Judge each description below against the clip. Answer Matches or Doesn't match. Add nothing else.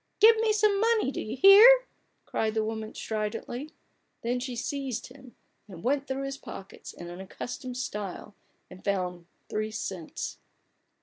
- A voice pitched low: Doesn't match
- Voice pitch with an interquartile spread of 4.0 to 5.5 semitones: Matches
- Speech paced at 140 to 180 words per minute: Matches